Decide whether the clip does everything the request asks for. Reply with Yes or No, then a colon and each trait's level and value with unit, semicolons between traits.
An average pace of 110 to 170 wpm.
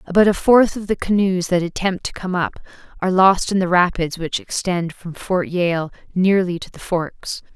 No: average, 200 wpm